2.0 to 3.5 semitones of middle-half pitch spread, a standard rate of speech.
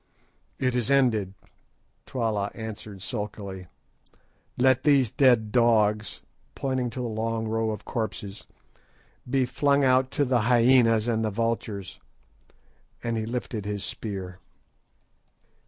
No: average, 3.0 semitones; slow, 120 wpm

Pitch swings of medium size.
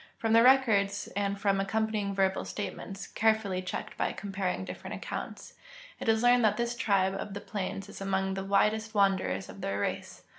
No: narrow, 2.2 semitones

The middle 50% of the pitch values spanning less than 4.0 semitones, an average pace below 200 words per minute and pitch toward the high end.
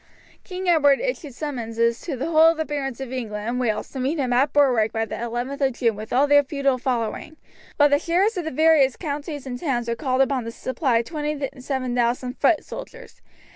No: average, 3.6 semitones; fast, 205 wpm; very high, 270 Hz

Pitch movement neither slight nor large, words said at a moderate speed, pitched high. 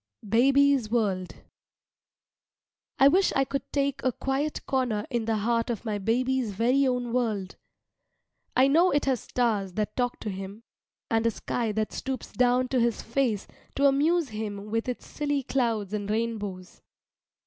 Yes: average, 3.9 semitones; average, 160 wpm; high, 235 Hz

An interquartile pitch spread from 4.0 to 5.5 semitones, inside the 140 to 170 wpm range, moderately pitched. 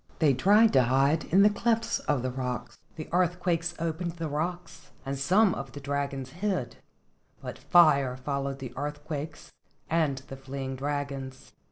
Yes: average, 4.3 semitones; average, 155 wpm; medium, 145 Hz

